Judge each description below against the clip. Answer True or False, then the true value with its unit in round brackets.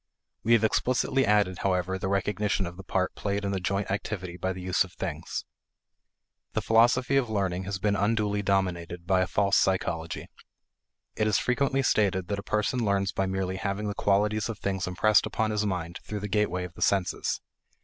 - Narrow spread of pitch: True (2.2 semitones)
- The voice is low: True (100 Hz)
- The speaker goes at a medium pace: True (190 wpm)